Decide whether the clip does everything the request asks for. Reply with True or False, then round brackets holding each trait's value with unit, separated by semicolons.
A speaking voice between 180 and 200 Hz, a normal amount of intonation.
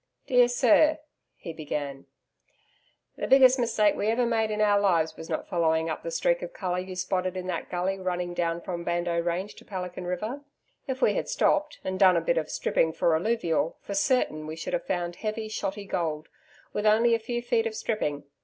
True (190 Hz; 5.0 semitones)